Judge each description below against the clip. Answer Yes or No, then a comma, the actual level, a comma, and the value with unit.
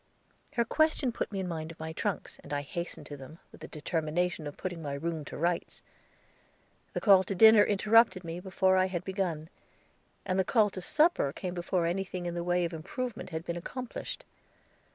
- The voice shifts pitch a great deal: No, average, 3.0 semitones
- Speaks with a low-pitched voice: No, medium, 180 Hz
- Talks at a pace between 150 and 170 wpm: No, average, 195 wpm